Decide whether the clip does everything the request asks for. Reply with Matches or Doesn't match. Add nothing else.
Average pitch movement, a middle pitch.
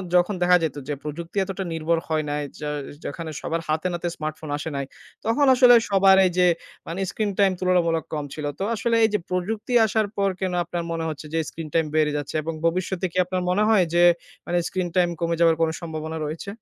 Matches